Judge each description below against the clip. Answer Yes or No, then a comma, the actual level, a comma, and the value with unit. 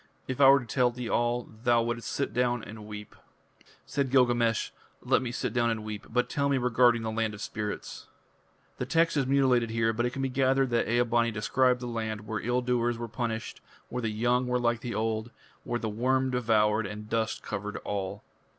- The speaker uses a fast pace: Yes, fast, 210 wpm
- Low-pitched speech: Yes, low, 120 Hz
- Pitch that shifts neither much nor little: No, narrow, 2.0 semitones